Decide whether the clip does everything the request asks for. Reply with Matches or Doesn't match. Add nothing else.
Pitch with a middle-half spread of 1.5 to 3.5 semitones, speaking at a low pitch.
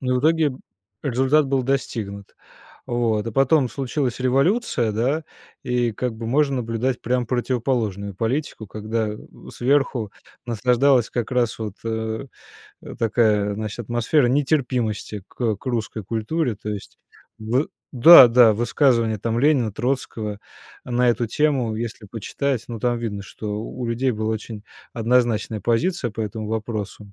Matches